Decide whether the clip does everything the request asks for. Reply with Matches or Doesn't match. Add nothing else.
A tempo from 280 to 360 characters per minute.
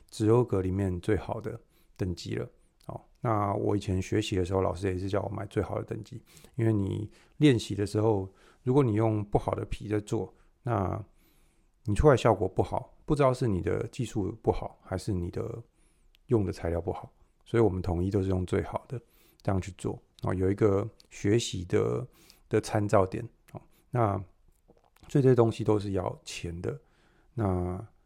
Doesn't match